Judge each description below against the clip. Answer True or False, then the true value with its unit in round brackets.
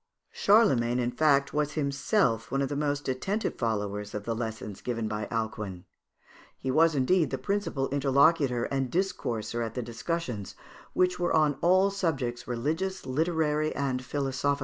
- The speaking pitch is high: False (135 Hz)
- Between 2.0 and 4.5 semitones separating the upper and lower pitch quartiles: False (5.3 semitones)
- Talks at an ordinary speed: True (150 wpm)